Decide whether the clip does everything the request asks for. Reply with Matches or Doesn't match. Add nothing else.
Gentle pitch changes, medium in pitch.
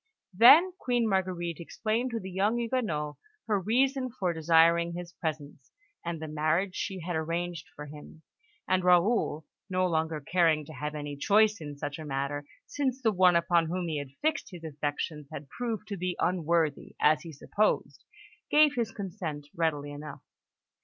Doesn't match